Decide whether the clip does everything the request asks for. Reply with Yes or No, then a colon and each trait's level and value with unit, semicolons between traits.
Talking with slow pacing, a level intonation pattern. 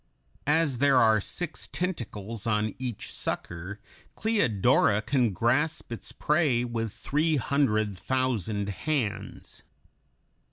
No: slow, 105 wpm; average, 5.1 semitones